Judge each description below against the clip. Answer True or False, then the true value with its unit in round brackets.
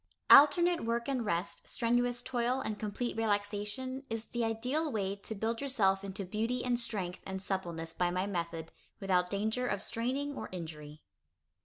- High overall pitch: True (220 Hz)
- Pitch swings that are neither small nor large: True (4.2 semitones)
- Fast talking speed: False (160 wpm)